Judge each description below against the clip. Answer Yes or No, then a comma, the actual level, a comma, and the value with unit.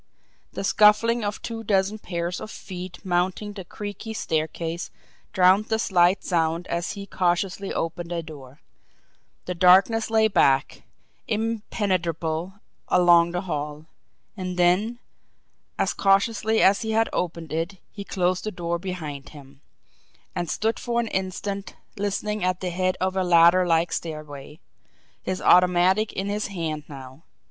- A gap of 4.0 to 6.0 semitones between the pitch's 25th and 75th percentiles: No, average, 3.3 semitones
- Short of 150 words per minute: Yes, average, 140 wpm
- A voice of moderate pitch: Yes, medium, 180 Hz